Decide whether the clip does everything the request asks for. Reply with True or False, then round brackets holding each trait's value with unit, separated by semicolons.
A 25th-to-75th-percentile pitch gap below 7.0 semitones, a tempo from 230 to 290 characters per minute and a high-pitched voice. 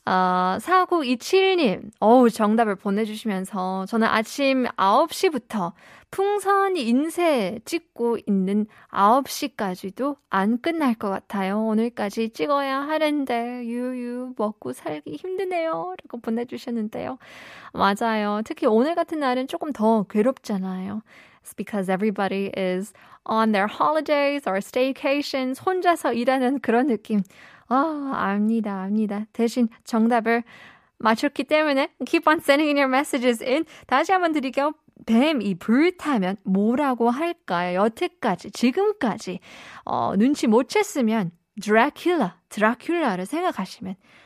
False (5.5 semitones; 345 characters per minute; 240 Hz)